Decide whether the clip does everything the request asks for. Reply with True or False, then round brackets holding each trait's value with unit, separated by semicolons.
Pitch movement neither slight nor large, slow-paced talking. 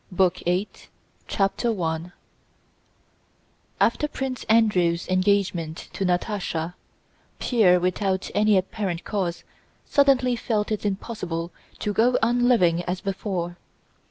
True (3.9 semitones; 115 wpm)